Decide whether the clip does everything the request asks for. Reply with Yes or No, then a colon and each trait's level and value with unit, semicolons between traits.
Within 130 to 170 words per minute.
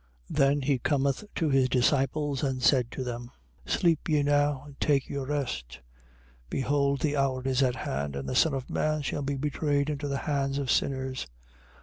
No: average, 190 wpm